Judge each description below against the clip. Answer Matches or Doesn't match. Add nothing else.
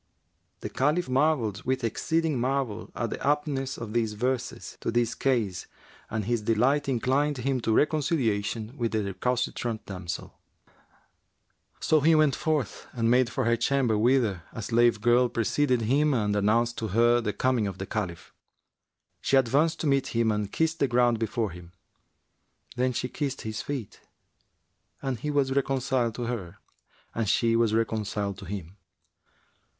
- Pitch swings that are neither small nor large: Matches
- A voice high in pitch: Doesn't match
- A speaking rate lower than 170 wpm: Matches